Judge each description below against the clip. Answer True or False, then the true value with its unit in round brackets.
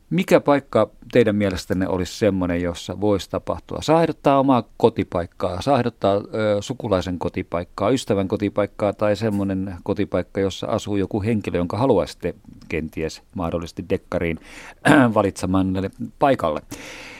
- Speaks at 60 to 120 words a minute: True (110 wpm)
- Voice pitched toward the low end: True (100 Hz)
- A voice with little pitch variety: False (3.5 semitones)